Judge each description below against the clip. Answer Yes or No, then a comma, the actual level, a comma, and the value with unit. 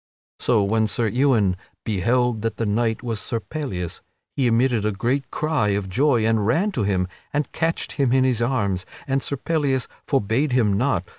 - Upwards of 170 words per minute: Yes, average, 180 wpm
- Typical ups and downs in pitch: Yes, average, 4.3 semitones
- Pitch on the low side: Yes, low, 120 Hz